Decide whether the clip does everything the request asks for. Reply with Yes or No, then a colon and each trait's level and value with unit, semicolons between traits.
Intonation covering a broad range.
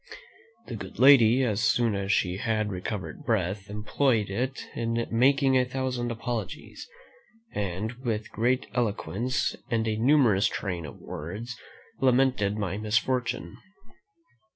No: average, 3.7 semitones